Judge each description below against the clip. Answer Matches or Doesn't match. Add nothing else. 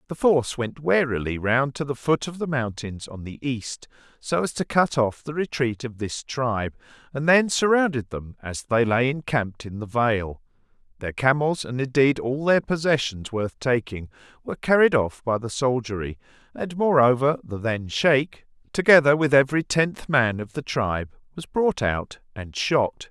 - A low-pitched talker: Matches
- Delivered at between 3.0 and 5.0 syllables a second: Matches